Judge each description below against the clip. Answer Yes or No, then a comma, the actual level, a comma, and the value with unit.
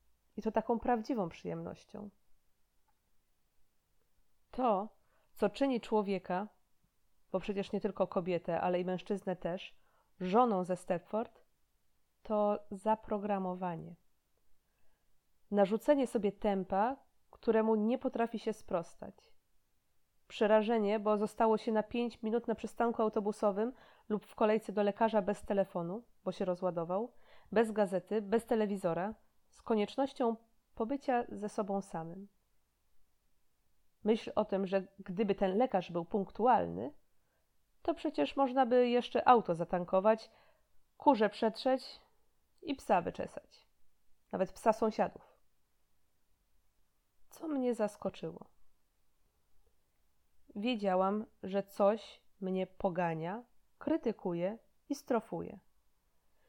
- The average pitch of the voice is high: Yes, high, 210 Hz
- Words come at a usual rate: No, slow, 100 wpm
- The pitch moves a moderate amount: Yes, average, 3.4 semitones